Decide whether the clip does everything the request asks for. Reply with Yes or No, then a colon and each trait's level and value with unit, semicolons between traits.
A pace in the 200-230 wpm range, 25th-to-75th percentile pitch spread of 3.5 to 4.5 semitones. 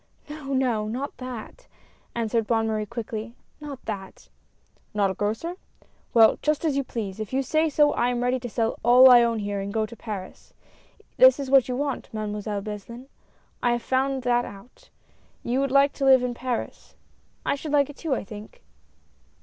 Yes: fast, 205 wpm; average, 3.9 semitones